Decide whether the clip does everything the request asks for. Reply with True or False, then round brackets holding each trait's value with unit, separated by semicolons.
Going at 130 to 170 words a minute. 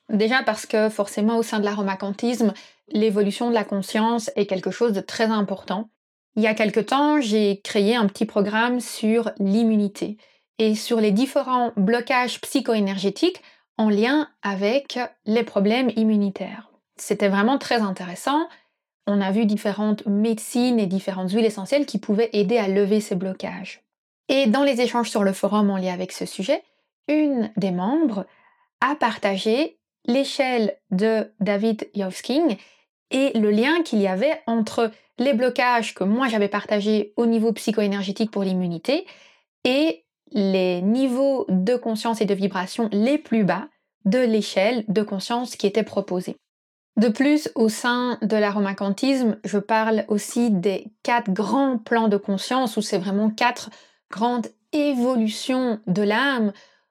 True (150 wpm)